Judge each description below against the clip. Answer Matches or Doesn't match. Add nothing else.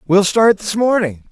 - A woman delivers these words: Doesn't match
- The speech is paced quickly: Doesn't match